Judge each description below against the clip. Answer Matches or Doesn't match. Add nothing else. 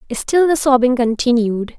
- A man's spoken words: Doesn't match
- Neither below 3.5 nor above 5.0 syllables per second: Matches